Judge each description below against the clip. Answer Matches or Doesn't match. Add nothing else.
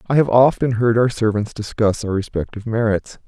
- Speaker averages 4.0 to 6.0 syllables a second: Matches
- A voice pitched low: Matches